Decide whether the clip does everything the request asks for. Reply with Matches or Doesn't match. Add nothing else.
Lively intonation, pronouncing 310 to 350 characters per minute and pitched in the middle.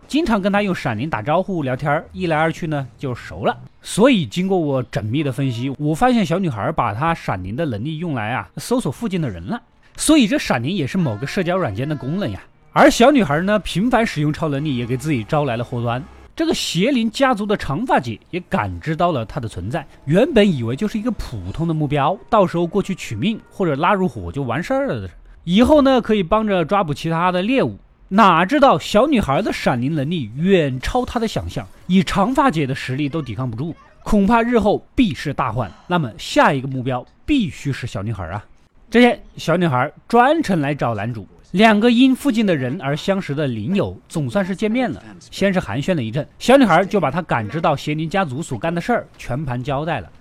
Matches